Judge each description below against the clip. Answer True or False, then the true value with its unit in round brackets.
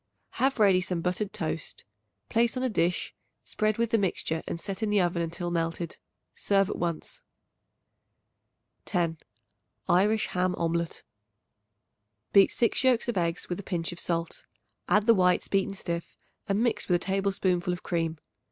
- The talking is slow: False (160 wpm)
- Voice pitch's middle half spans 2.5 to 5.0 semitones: True (3.4 semitones)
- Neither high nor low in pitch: True (180 Hz)